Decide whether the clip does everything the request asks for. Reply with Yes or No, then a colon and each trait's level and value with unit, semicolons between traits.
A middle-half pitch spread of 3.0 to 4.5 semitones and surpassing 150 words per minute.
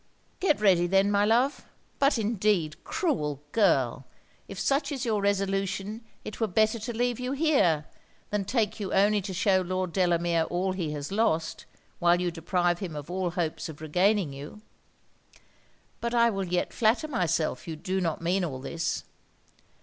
Yes: average, 4.1 semitones; average, 165 wpm